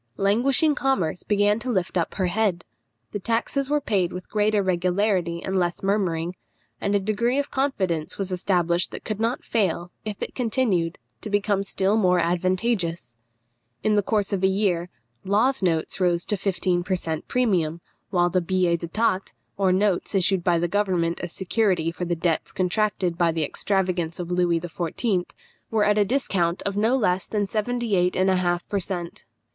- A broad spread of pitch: No, average, 3.2 semitones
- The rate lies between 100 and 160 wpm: No, average, 175 wpm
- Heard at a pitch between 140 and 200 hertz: Yes, high, 190 Hz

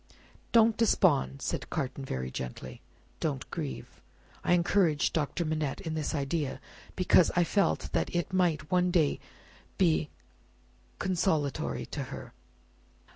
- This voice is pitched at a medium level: Yes, medium, 160 Hz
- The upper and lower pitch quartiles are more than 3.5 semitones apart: Yes, average, 4.2 semitones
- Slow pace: Yes, slow, 125 wpm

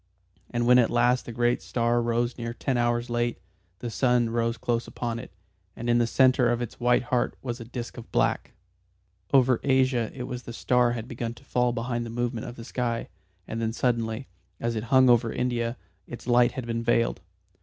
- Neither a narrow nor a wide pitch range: No, narrow, 1.1 semitones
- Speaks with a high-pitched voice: No, low, 120 Hz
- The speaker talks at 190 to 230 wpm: Yes, fast, 205 wpm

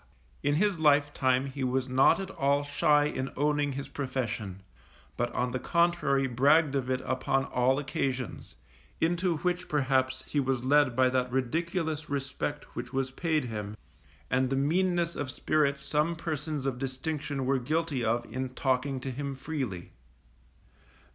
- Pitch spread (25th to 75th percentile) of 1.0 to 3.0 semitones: Yes, narrow, 2.6 semitones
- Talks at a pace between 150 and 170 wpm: Yes, average, 155 wpm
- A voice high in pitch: No, low, 135 Hz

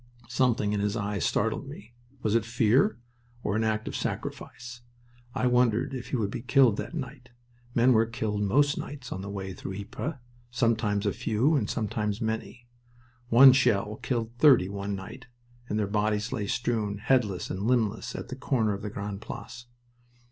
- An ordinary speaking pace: Yes, average, 175 wpm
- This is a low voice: Yes, low, 110 Hz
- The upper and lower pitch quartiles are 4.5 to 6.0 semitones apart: No, average, 3.2 semitones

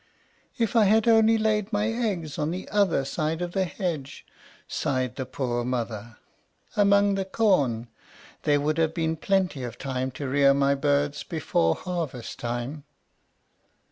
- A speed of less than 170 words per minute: Yes, average, 150 wpm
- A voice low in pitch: No, medium, 155 Hz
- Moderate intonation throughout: No, wide, 6.8 semitones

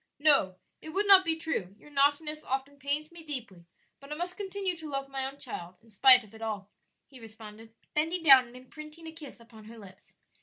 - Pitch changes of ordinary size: No, wide, 5.8 semitones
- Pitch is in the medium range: No, very high, 275 Hz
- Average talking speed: No, fast, 215 wpm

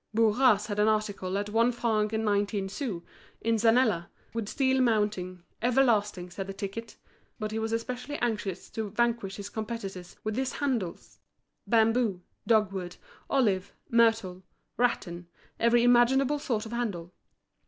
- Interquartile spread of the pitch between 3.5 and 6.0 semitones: No, average, 3.1 semitones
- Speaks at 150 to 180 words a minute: No, slow, 135 wpm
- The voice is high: Yes, high, 220 Hz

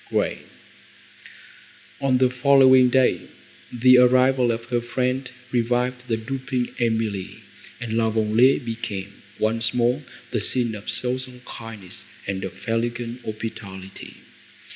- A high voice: No, low, 120 Hz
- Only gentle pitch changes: Yes, narrow, 2.2 semitones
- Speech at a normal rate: No, slow, 120 wpm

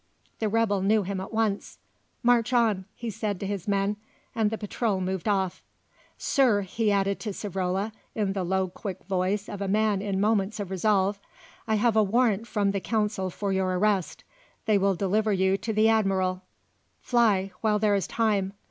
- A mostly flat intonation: Yes, narrow, 2.3 semitones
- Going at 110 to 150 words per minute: No, average, 185 wpm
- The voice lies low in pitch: No, high, 205 Hz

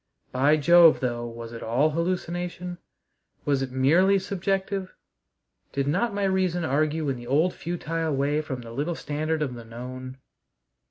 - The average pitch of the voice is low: No, medium, 155 Hz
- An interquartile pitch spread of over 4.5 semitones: Yes, average, 5.1 semitones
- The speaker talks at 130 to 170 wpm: Yes, average, 155 wpm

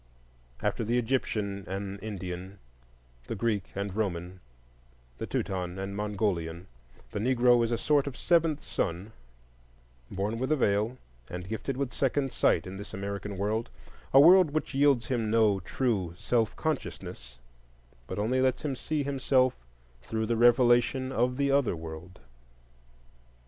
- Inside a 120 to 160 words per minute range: Yes, average, 140 wpm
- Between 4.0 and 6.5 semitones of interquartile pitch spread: Yes, average, 5.0 semitones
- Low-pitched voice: Yes, low, 110 Hz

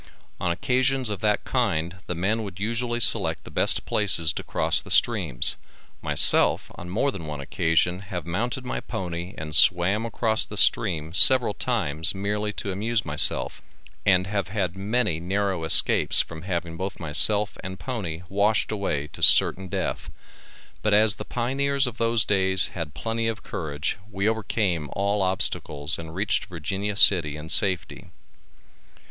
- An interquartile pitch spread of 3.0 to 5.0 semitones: Yes, average, 4.3 semitones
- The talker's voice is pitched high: No, very low, 95 Hz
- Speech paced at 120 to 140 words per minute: No, average, 155 wpm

